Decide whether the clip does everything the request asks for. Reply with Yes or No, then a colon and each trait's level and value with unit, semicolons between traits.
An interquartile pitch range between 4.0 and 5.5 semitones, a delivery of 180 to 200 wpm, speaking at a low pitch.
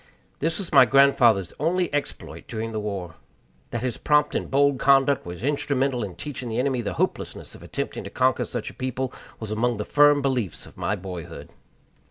Yes: average, 4.6 semitones; average, 190 wpm; low, 125 Hz